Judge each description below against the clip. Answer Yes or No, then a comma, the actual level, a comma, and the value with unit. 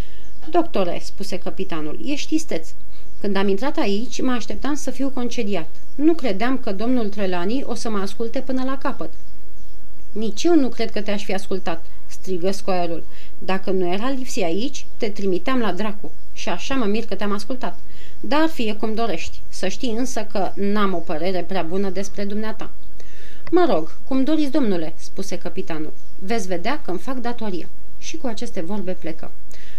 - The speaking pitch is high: Yes, high, 210 Hz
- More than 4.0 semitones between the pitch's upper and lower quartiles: Yes, wide, 5.4 semitones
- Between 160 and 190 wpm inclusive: Yes, fast, 170 wpm